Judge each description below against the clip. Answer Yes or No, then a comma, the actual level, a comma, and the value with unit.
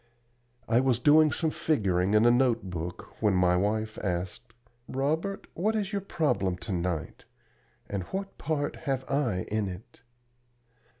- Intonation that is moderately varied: No, wide, 8.2 semitones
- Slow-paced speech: No, average, 145 wpm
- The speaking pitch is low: Yes, low, 115 Hz